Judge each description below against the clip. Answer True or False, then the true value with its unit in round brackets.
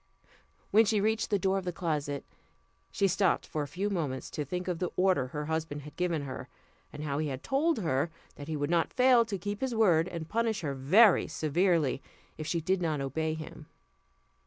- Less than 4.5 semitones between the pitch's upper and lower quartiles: False (4.9 semitones)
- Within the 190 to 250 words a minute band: True (205 wpm)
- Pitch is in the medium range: True (170 Hz)